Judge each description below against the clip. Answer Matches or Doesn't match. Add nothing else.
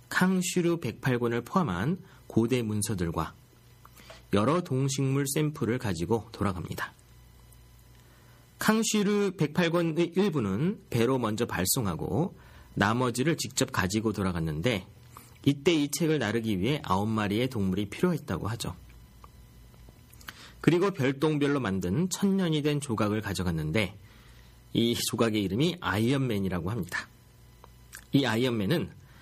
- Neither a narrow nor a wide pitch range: Doesn't match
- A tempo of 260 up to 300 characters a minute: Matches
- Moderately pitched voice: Doesn't match